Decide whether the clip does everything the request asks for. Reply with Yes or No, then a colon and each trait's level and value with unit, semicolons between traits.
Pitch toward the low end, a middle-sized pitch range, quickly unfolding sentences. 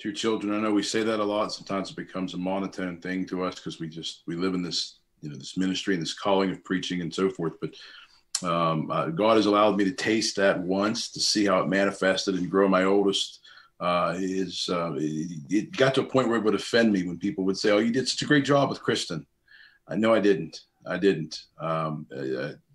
Yes: very low, 95 Hz; average, 3.0 semitones; fast, 245 wpm